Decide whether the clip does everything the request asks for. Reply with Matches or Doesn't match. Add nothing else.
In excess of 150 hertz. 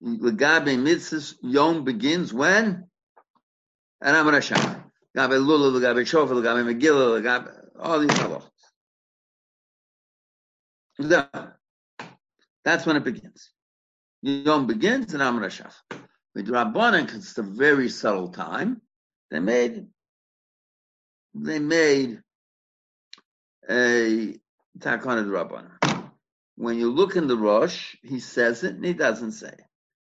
Doesn't match